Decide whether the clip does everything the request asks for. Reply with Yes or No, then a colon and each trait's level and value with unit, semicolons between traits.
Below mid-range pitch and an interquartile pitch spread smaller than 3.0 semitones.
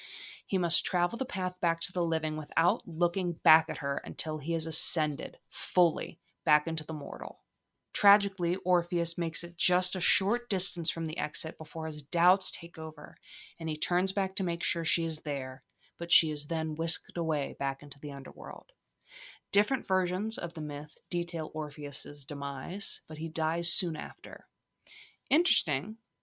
No: medium, 165 Hz; narrow, 2.5 semitones